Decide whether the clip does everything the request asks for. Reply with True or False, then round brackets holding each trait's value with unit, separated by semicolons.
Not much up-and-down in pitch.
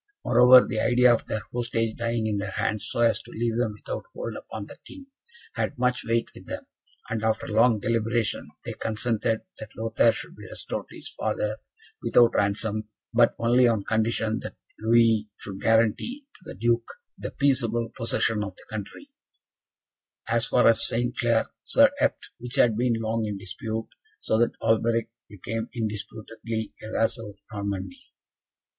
True (1.5 semitones)